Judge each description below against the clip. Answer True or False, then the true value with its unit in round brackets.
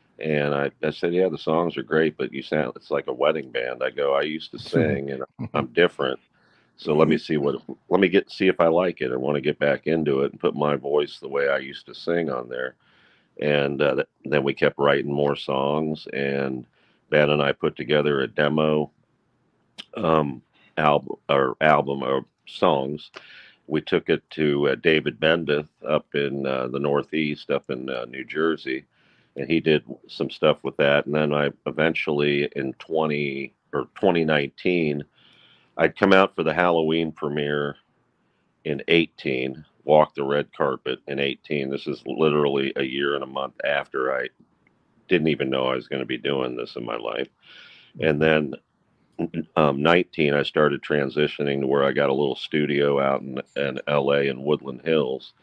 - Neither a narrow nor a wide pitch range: False (1.9 semitones)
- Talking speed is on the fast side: False (185 wpm)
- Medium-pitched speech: False (75 Hz)